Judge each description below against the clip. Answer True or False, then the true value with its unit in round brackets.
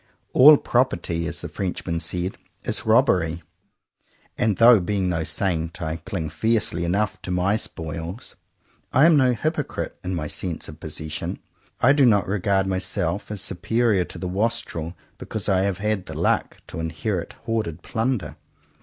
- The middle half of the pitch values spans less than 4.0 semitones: False (4.6 semitones)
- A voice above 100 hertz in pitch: False (95 Hz)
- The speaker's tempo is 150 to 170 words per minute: True (160 wpm)